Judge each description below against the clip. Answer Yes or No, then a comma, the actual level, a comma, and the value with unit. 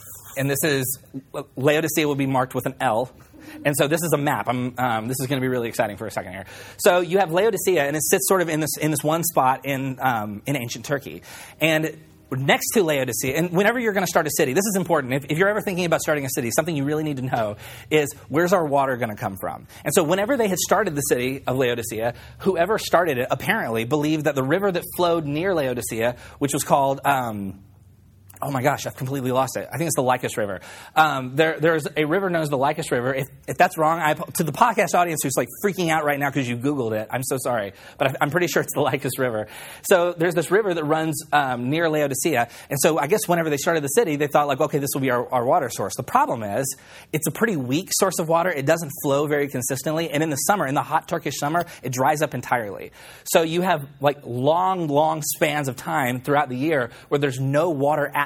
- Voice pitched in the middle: Yes, medium, 145 Hz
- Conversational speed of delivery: No, fast, 245 wpm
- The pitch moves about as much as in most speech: Yes, average, 4.0 semitones